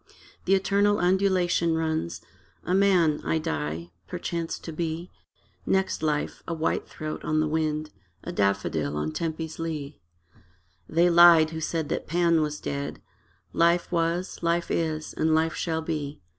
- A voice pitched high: No, medium, 160 Hz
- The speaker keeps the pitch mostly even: Yes, narrow, 2.0 semitones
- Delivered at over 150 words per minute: No, average, 145 wpm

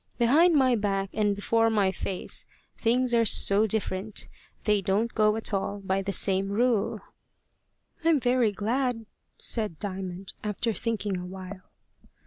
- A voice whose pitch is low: No, high, 210 Hz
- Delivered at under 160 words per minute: Yes, average, 140 wpm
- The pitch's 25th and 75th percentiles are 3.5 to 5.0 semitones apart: No, average, 3.0 semitones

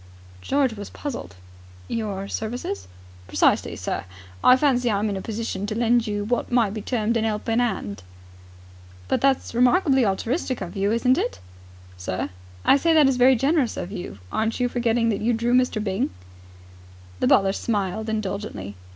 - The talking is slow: No, average, 170 wpm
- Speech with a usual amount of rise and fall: Yes, average, 3.6 semitones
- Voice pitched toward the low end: No, high, 225 Hz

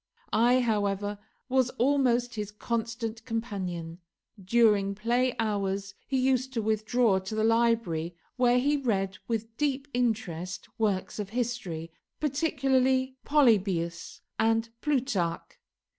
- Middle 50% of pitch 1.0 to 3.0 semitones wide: No, average, 4.1 semitones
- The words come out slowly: Yes, slow, 115 wpm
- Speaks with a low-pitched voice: No, high, 225 Hz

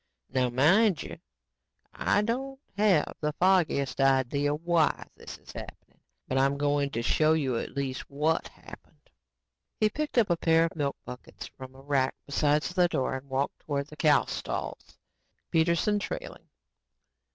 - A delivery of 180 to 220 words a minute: No, average, 155 wpm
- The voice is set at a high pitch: No, medium, 150 Hz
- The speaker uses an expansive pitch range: No, average, 4.2 semitones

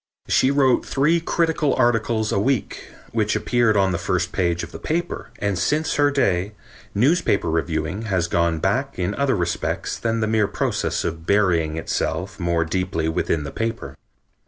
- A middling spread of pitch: No, wide, 6.4 semitones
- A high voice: No, low, 100 Hz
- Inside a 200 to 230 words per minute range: No, average, 165 wpm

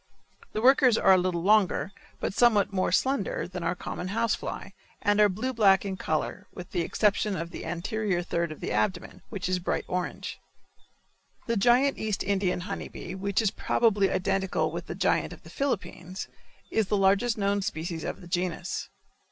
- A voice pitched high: Yes, high, 195 Hz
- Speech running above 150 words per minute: Yes, average, 185 wpm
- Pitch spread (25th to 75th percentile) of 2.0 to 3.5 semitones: Yes, average, 3.1 semitones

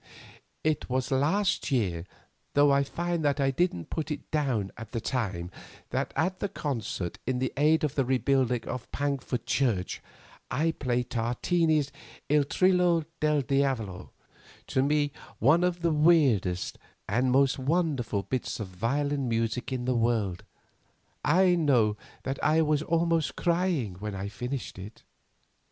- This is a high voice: No, low, 135 Hz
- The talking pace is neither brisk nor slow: Yes, average, 145 wpm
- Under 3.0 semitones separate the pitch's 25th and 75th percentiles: No, average, 4.8 semitones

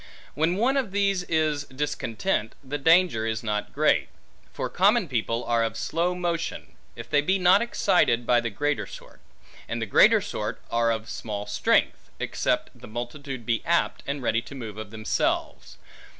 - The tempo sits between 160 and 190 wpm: Yes, average, 170 wpm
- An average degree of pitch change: No, wide, 7.2 semitones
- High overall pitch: No, medium, 140 Hz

